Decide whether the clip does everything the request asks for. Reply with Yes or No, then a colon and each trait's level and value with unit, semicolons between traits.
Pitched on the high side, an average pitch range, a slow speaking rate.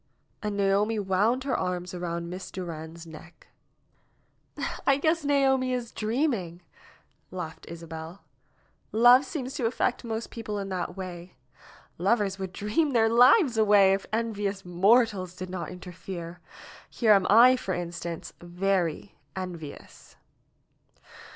Yes: high, 195 Hz; average, 4.7 semitones; slow, 125 wpm